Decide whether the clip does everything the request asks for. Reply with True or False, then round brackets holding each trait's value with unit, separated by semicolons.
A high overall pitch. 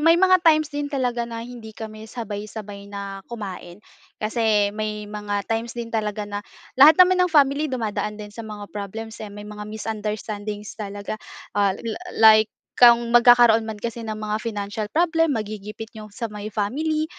True (220 Hz)